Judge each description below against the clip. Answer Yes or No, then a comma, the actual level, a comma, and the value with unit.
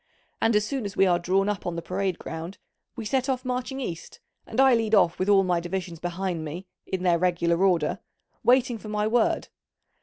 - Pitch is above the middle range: Yes, high, 195 Hz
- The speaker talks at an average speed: No, fast, 210 wpm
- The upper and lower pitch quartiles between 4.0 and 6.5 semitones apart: Yes, average, 4.4 semitones